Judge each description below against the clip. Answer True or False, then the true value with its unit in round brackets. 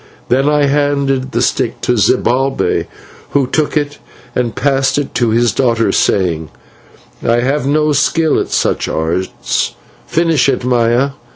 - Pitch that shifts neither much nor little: True (3.3 semitones)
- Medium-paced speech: True (150 wpm)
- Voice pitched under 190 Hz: True (135 Hz)